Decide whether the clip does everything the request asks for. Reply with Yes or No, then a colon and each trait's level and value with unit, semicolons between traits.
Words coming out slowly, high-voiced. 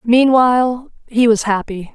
Yes: slow, 125 wpm; high, 235 Hz